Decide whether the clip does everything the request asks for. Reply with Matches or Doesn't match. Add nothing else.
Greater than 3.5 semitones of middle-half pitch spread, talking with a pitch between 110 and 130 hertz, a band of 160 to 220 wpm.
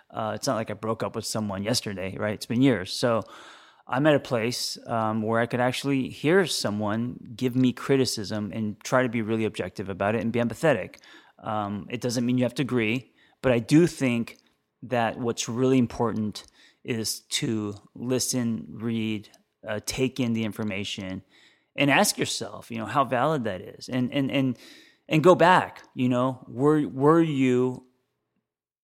Doesn't match